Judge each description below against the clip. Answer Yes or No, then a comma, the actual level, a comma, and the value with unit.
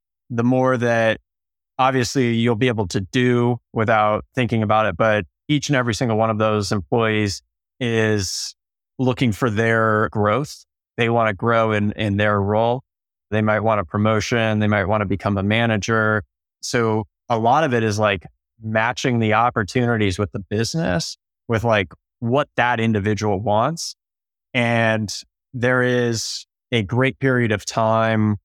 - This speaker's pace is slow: No, average, 155 wpm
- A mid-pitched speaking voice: No, low, 110 Hz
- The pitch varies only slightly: Yes, narrow, 2.3 semitones